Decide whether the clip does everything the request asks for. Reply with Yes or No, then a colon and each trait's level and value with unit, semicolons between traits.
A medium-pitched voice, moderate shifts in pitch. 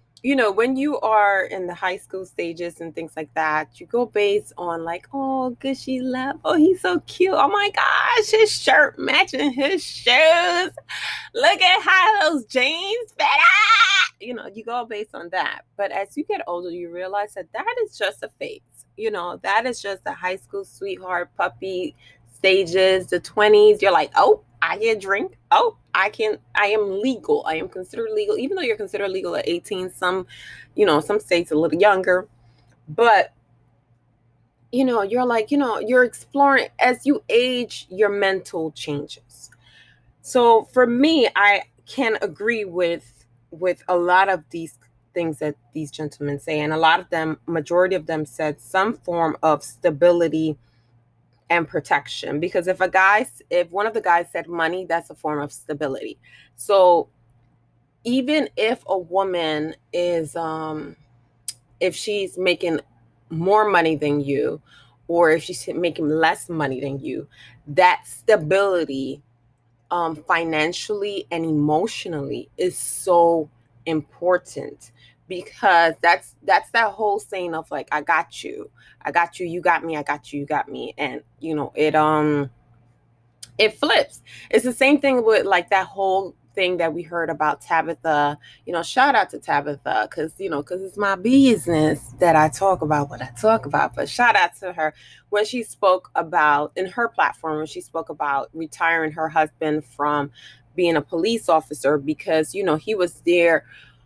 No: medium, 175 Hz; wide, 6.5 semitones